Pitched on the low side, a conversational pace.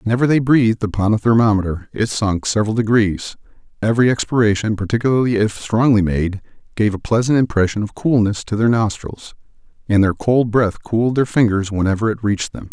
Yes: low, 110 Hz; average, 170 wpm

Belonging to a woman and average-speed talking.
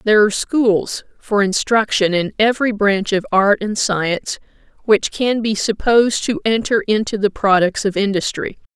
Yes: female; average, 160 wpm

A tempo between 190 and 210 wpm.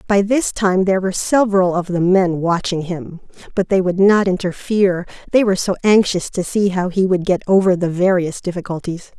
Yes: average, 195 wpm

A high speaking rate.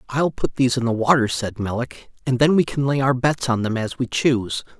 Yes: fast, 250 wpm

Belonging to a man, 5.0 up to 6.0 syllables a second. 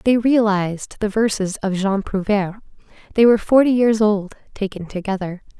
No: female; 5.3 syllables/s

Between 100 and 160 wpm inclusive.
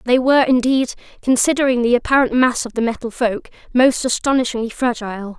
Yes: average, 155 wpm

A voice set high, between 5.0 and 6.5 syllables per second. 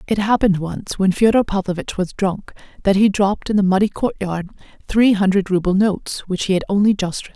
Yes: high, 195 Hz; 6.0 syllables/s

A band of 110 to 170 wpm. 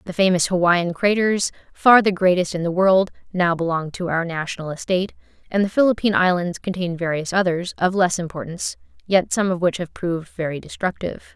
No: average, 180 wpm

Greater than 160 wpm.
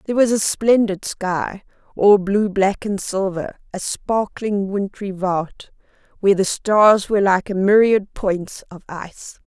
No: average, 145 wpm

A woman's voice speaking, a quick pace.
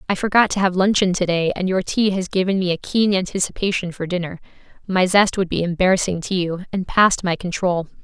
Yes: female; fast, 215 wpm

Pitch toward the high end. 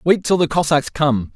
No: medium, 145 Hz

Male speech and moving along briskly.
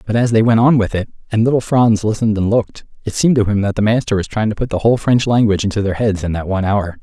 Yes: male; fast, 300 wpm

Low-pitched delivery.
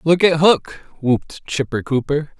No: medium, 150 Hz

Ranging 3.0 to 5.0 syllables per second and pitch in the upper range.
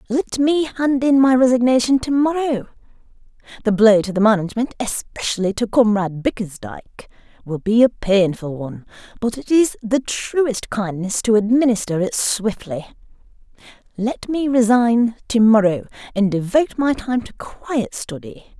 Yes: 4.7 syllables/s; high, 230 Hz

